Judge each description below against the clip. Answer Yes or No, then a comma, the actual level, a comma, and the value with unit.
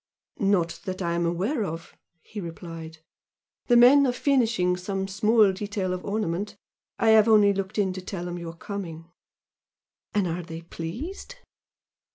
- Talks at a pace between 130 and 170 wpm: Yes, average, 160 wpm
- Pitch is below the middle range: No, high, 190 Hz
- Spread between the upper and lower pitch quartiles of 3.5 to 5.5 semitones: Yes, average, 3.9 semitones